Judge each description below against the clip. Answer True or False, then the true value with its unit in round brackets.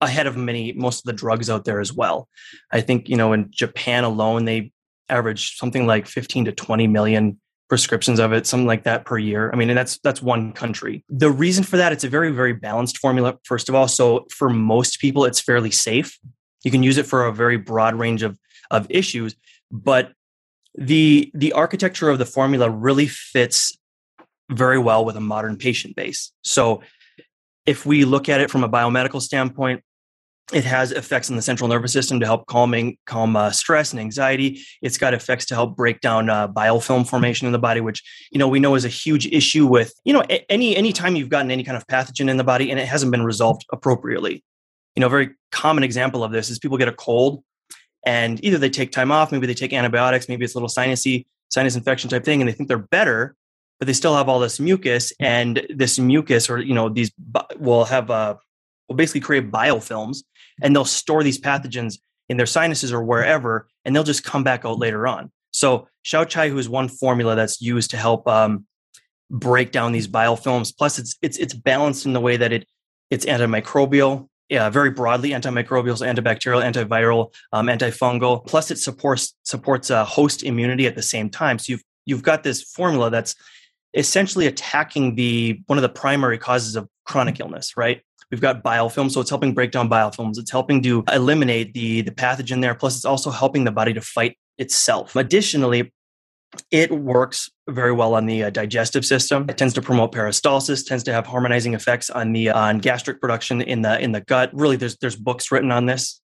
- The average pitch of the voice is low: True (125 Hz)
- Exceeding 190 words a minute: True (205 wpm)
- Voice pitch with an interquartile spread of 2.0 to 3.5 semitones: True (2.8 semitones)